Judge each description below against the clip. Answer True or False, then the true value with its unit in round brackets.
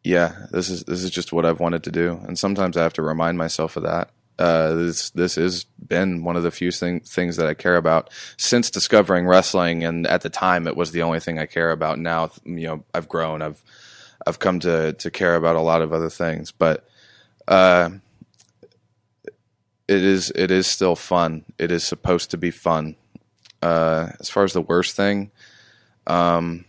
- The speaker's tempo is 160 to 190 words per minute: False (200 wpm)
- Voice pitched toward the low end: True (85 Hz)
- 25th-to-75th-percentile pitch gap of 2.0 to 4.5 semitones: False (1.5 semitones)